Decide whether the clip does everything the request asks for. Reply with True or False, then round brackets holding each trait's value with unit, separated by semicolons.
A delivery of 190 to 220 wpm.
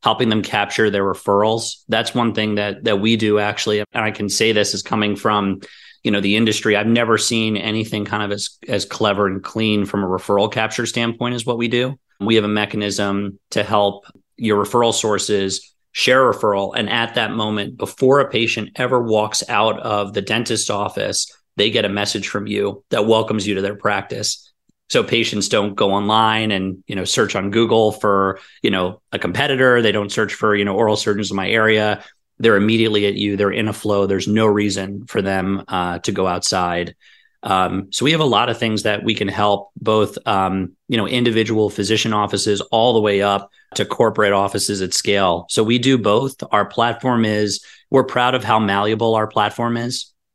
True (200 wpm)